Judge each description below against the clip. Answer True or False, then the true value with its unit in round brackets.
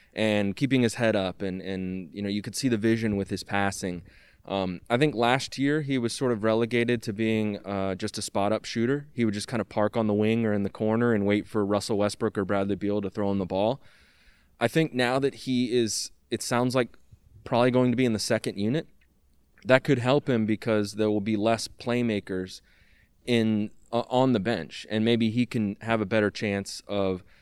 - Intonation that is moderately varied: True (3.2 semitones)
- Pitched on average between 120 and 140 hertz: False (110 Hz)